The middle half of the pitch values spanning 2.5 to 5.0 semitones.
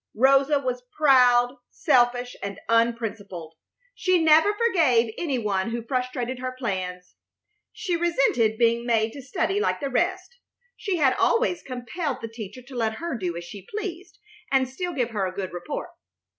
No: wide, 5.4 semitones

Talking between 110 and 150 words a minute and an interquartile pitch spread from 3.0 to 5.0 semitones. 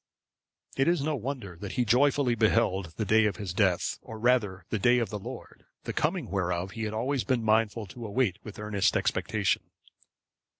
No: average, 185 wpm; average, 3.8 semitones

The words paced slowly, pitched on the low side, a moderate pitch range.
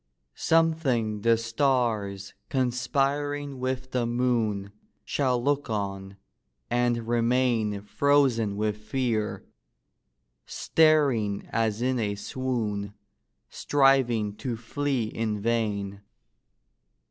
Yes: slow, 90 wpm; low, 120 Hz; average, 3.6 semitones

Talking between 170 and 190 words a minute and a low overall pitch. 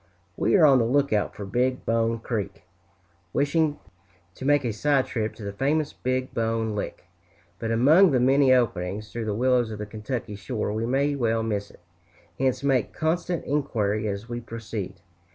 Yes: average, 175 wpm; low, 120 Hz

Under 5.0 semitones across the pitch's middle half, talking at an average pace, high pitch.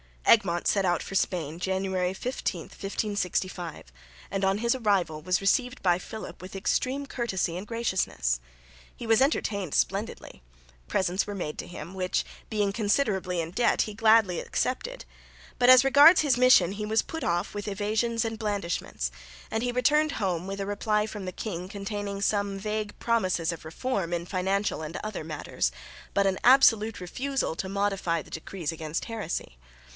Yes: average, 3.8 semitones; average, 165 wpm; high, 200 Hz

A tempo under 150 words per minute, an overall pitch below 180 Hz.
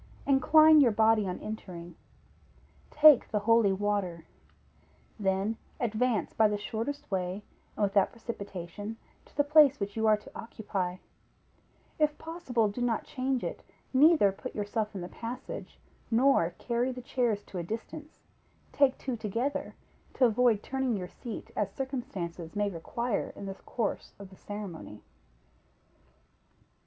No: average, 140 wpm; high, 220 Hz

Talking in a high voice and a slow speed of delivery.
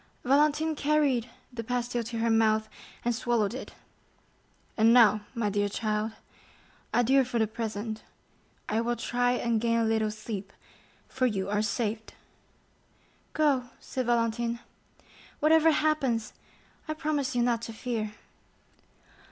Yes: high, 235 Hz; slow, 130 wpm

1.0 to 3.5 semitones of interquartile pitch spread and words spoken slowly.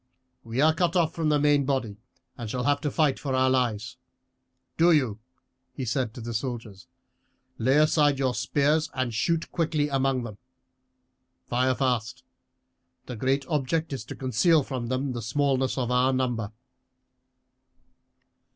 No: average, 3.2 semitones; average, 150 wpm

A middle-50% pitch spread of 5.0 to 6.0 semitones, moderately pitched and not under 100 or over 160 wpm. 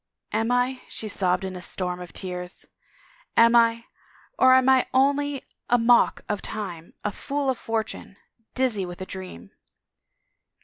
No: wide, 5.4 semitones; high, 225 Hz; average, 150 wpm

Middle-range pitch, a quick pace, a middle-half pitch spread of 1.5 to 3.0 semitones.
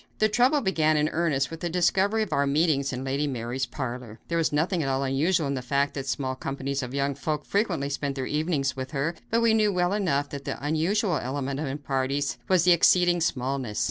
No: medium, 145 Hz; fast, 225 wpm; average, 4.3 semitones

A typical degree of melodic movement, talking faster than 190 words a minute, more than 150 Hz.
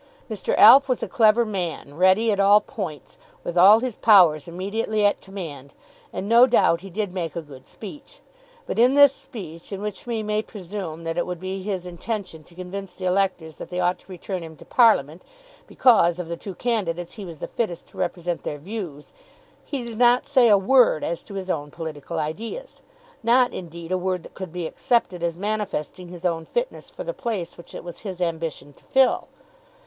Yes: average, 4.5 semitones; fast, 205 wpm; high, 190 Hz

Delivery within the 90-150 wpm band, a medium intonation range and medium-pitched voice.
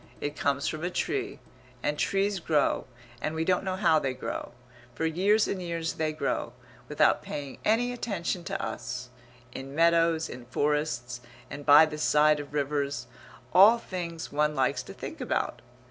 No: average, 165 wpm; average, 4.1 semitones; medium, 155 Hz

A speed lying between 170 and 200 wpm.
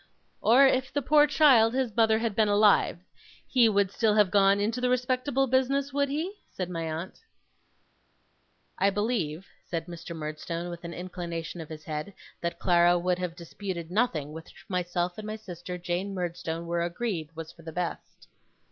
Yes: average, 175 wpm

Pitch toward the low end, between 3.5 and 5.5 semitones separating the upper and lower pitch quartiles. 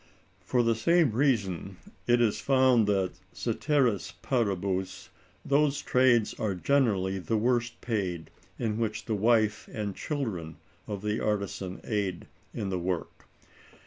Yes: low, 110 Hz; average, 4.1 semitones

